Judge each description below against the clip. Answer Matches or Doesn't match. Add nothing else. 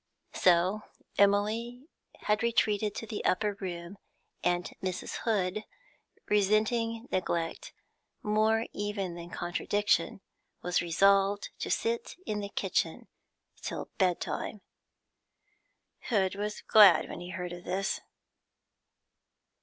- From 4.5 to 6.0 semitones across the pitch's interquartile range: Doesn't match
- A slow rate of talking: Matches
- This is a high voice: Matches